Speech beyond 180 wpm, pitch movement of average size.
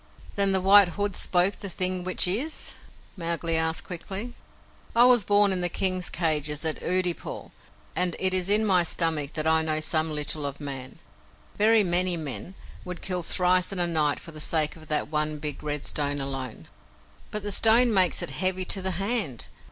Yes: average, 190 wpm; average, 3.7 semitones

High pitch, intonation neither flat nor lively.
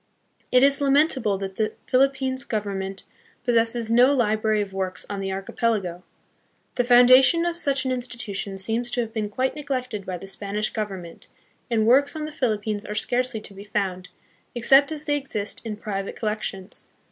Yes: high, 225 Hz; average, 4.3 semitones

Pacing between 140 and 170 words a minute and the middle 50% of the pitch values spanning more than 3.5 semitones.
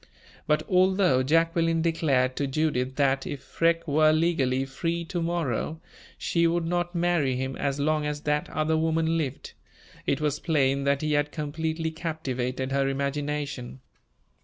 No: average, 150 wpm; average, 3.2 semitones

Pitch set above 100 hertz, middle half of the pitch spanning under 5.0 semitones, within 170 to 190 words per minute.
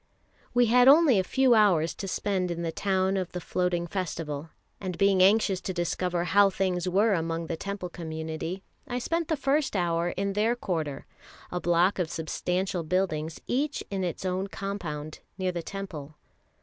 Yes: medium, 185 Hz; average, 2.9 semitones; average, 175 wpm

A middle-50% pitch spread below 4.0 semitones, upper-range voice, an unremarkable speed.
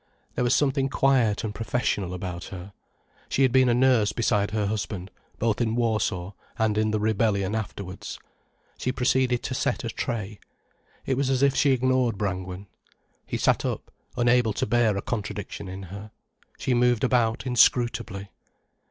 No: average, 3.5 semitones; low, 110 Hz; average, 160 wpm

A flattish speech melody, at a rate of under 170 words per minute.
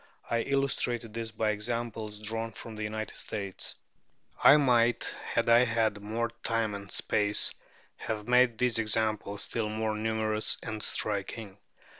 Yes: narrow, 1.5 semitones; average, 140 wpm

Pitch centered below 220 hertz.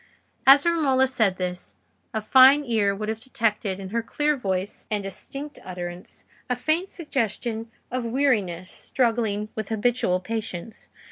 No: high, 225 Hz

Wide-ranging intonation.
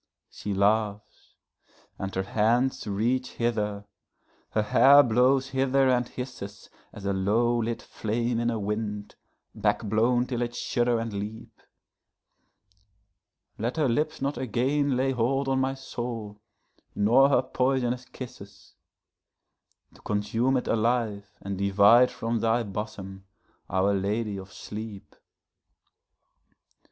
No: average, 3.5 semitones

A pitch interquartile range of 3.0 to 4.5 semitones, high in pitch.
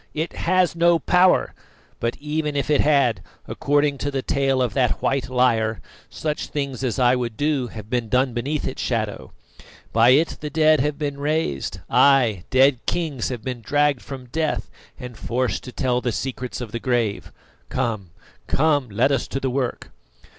No: average, 3.3 semitones; low, 130 Hz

